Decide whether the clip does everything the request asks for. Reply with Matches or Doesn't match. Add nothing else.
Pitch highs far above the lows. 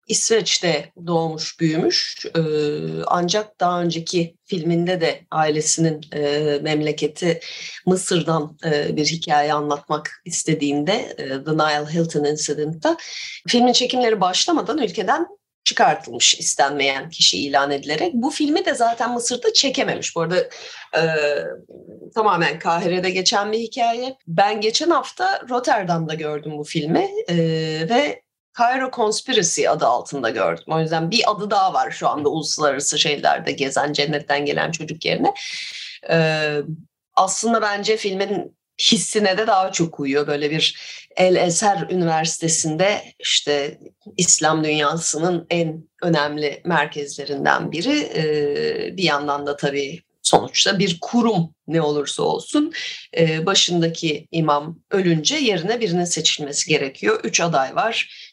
Matches